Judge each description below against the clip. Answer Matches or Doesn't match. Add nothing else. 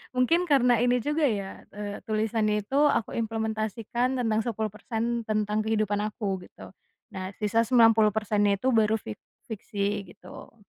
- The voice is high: Matches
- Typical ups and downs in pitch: Doesn't match